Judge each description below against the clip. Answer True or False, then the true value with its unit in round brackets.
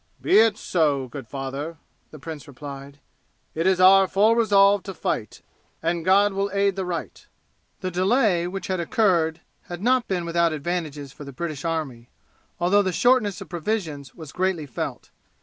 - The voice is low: False (175 Hz)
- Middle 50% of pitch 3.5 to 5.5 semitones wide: True (4.6 semitones)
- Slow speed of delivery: False (165 wpm)